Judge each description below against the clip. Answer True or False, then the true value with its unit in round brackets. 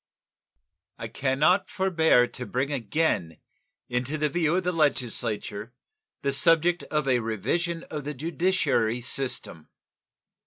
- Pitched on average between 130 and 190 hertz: True (140 Hz)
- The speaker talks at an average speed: False (125 wpm)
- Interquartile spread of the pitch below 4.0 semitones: False (5.2 semitones)